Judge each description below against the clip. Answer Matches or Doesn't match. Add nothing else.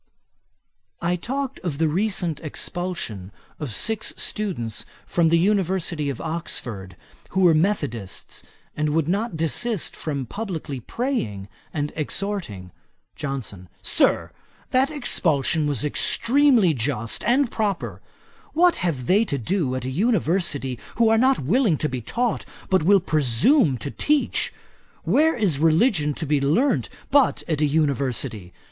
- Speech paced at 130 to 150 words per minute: Matches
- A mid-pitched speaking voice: Matches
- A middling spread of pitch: Doesn't match